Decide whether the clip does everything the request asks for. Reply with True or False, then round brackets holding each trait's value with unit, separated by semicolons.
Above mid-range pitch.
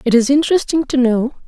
True (265 Hz)